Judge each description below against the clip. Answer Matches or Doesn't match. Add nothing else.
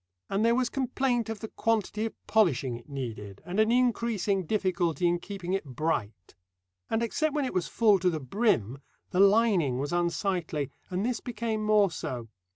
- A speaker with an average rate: Matches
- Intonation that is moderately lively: Doesn't match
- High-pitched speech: Matches